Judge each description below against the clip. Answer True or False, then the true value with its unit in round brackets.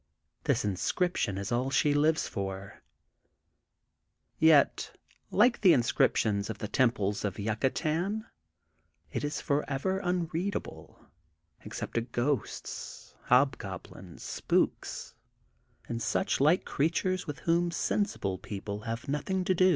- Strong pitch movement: True (8.5 semitones)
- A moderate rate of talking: False (110 wpm)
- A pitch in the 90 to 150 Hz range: True (140 Hz)